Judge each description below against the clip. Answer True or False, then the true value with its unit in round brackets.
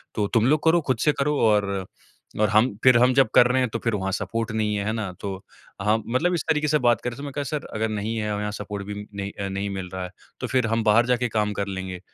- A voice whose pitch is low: True (110 Hz)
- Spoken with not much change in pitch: False (3.5 semitones)